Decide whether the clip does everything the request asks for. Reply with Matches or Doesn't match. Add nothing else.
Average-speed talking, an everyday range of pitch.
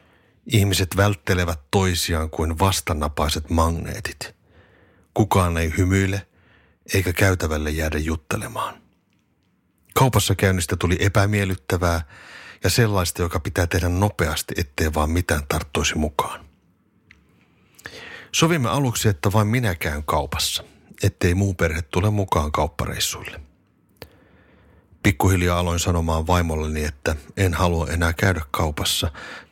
Matches